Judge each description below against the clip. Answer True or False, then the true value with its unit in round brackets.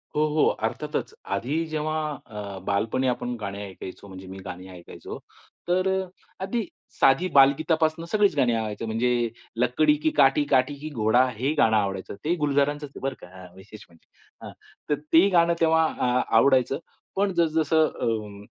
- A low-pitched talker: True (130 Hz)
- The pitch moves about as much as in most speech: False (6.6 semitones)